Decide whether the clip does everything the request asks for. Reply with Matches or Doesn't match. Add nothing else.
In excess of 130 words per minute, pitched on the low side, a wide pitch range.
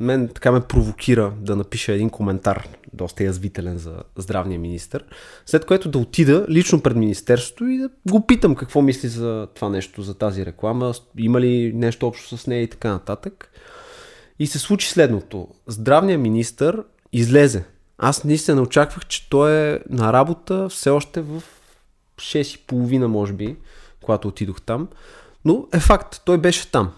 Matches